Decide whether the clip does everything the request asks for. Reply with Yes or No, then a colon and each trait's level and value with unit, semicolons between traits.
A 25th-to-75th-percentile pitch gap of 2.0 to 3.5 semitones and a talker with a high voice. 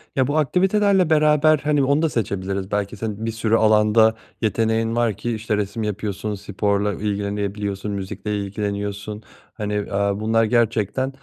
No: narrow, 2.5 semitones; low, 105 Hz